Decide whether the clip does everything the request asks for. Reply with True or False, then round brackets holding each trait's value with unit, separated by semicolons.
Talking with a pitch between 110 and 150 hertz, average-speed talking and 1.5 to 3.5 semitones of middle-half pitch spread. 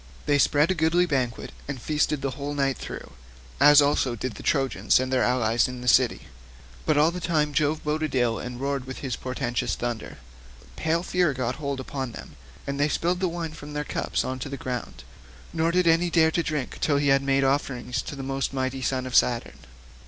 False (140 Hz; 210 wpm; 3.1 semitones)